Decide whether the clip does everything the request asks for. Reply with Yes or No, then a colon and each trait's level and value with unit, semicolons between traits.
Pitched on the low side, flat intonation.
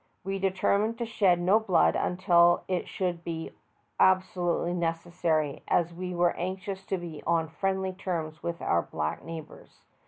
No: medium, 175 Hz; narrow, 2.2 semitones